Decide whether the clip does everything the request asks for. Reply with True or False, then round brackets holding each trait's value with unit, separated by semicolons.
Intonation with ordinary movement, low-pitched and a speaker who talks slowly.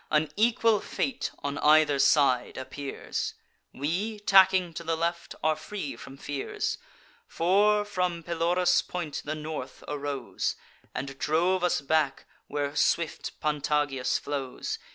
False (4.0 semitones; 155 Hz; 125 wpm)